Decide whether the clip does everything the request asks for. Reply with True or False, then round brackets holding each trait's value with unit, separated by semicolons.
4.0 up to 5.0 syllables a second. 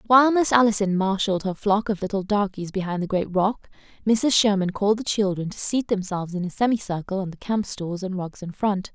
False (5.7 syllables/s)